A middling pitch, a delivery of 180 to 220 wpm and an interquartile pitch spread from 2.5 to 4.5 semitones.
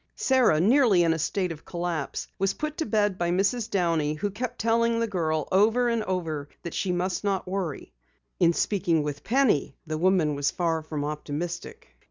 No: medium, 180 Hz; average, 185 wpm; average, 5.3 semitones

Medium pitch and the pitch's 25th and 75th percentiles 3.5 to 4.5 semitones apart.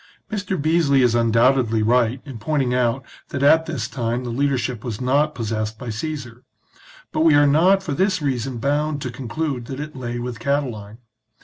No: low, 130 Hz; average, 3.9 semitones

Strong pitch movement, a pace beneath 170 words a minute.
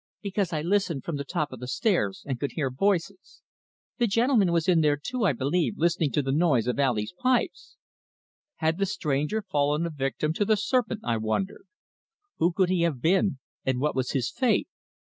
No: wide, 6.3 semitones; average, 195 wpm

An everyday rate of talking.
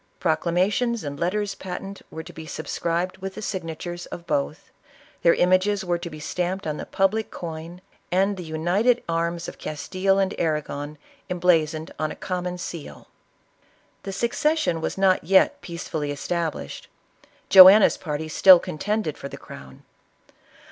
Yes: average, 150 wpm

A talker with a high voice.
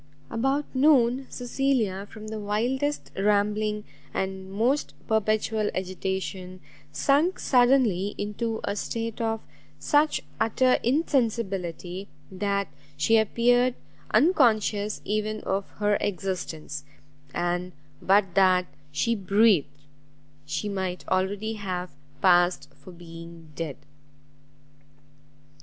Yes: high, 205 Hz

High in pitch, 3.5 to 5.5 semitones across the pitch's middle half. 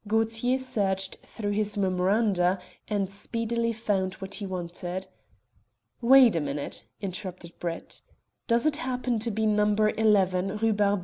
No: high, 205 Hz; average, 3.1 semitones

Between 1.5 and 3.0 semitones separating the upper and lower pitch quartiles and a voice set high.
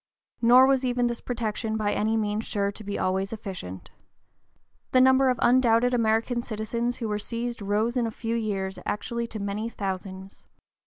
Yes: narrow, 2.6 semitones; high, 225 Hz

